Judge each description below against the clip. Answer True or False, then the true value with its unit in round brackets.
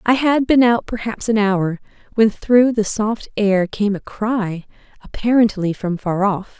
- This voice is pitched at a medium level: False (215 Hz)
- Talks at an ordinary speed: True (175 wpm)